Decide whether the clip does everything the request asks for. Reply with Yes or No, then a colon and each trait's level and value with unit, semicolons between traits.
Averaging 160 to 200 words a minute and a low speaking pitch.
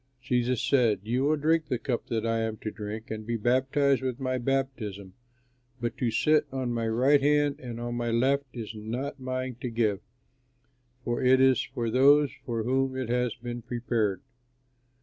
Yes: average, 180 wpm; low, 125 Hz